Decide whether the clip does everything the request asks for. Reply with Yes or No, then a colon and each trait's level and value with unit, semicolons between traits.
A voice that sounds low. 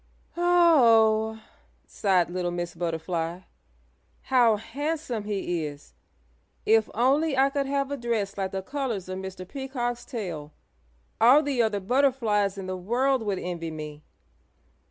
No: high, 220 Hz